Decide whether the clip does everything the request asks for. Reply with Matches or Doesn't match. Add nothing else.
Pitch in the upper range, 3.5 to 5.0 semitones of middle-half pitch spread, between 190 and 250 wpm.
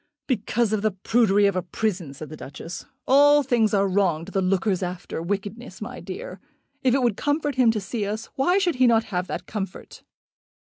Matches